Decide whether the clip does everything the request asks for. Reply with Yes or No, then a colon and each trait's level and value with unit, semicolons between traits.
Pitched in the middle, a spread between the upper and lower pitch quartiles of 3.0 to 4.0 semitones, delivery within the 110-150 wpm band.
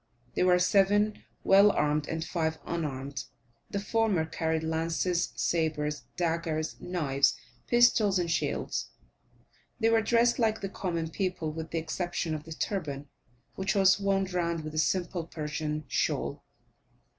Yes: medium, 170 Hz; average, 3.6 semitones; average, 140 wpm